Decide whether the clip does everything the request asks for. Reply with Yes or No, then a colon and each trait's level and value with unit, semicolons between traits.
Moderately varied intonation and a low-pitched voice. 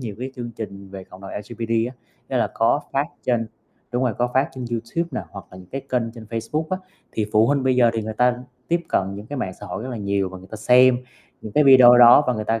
Yes: average, 3.3 semitones; low, 115 Hz